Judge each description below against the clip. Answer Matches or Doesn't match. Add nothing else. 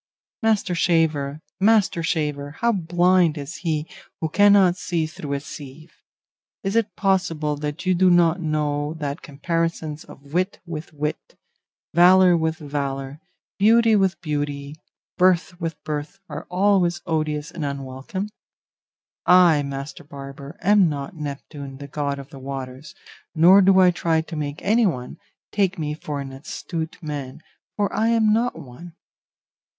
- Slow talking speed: Doesn't match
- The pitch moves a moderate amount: Matches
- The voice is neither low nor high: Matches